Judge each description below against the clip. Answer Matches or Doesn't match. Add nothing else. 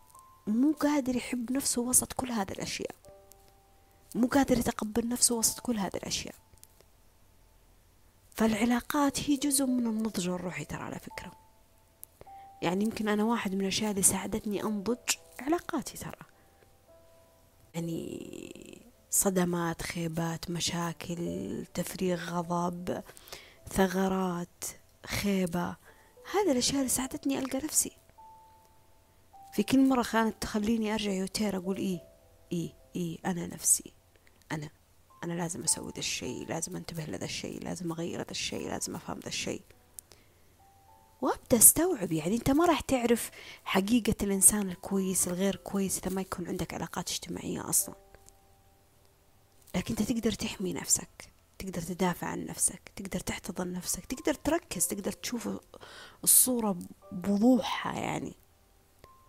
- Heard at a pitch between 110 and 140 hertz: Doesn't match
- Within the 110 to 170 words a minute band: Matches